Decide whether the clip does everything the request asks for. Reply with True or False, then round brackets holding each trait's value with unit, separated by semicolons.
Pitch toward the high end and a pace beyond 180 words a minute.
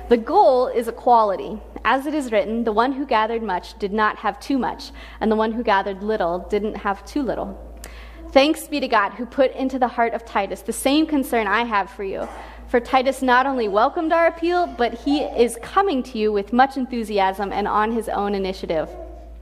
True (235 Hz; 205 wpm)